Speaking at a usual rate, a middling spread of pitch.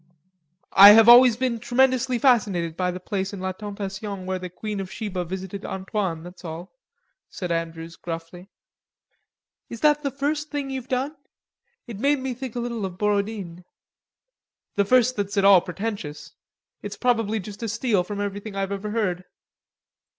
Yes: average, 165 wpm; average, 4.5 semitones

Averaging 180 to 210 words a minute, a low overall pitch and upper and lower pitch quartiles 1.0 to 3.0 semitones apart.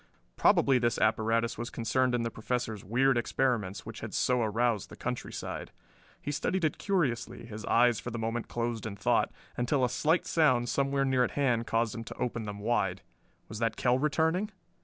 Yes: average, 185 wpm; low, 120 Hz; average, 2.7 semitones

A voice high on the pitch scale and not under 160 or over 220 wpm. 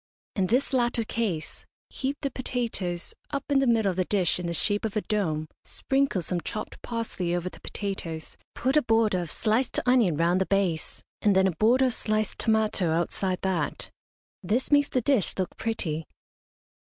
Yes: high, 210 Hz; average, 180 wpm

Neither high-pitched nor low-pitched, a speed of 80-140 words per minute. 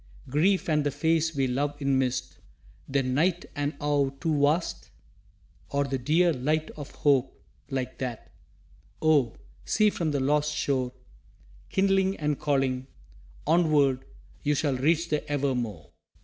Yes: medium, 145 Hz; slow, 135 wpm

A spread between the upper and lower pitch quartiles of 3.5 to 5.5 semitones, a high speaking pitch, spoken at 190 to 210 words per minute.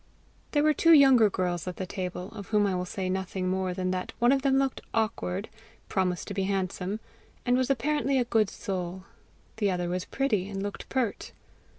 Yes: average, 5.0 semitones; high, 195 Hz; average, 200 wpm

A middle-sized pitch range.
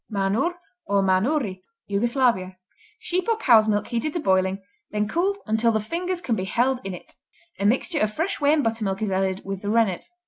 No: wide, 6.6 semitones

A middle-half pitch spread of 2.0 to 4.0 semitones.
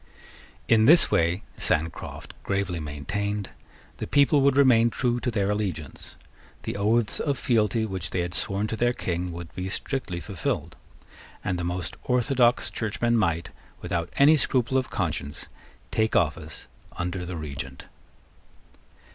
No: wide, 5.5 semitones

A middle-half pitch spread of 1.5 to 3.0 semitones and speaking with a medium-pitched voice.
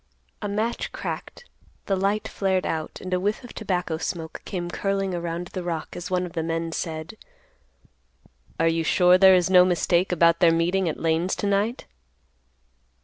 Yes: narrow, 2.5 semitones; medium, 180 Hz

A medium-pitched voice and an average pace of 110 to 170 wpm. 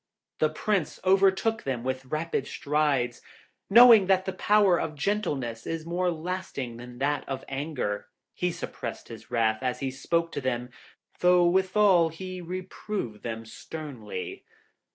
Yes: medium, 155 Hz; average, 145 wpm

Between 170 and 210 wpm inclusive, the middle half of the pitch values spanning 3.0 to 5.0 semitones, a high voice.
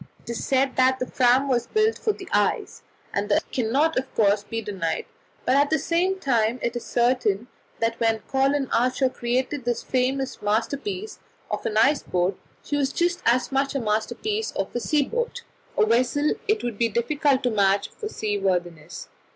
Yes: average, 185 wpm; average, 4.3 semitones; very high, 255 Hz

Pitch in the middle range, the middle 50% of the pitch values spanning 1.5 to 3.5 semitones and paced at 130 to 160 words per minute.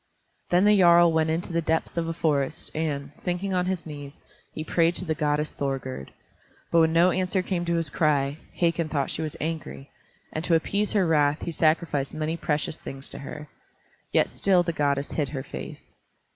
No: medium, 160 Hz; average, 2.8 semitones; average, 195 wpm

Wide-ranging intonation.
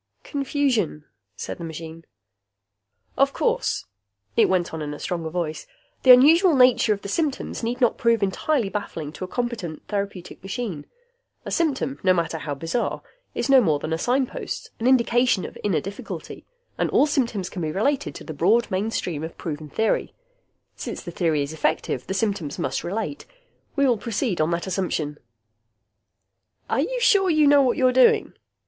Yes: wide, 7.6 semitones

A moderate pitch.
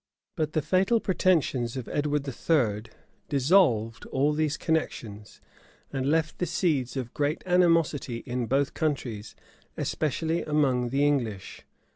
Yes: medium, 145 Hz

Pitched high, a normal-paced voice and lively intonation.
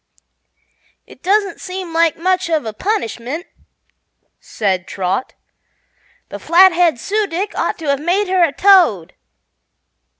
No: very high, 340 Hz; slow, 125 wpm; wide, 6.1 semitones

